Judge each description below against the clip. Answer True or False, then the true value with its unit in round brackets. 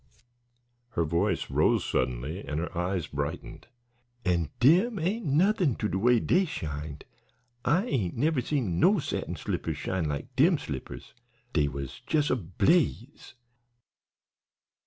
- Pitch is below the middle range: True (105 Hz)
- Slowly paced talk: True (130 wpm)